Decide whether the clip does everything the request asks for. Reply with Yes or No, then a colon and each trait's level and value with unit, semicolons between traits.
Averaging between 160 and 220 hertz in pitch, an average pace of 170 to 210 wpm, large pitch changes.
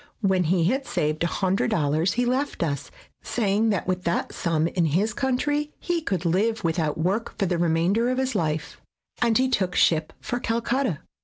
Yes: high, 190 Hz; average, 175 wpm; wide, 6.4 semitones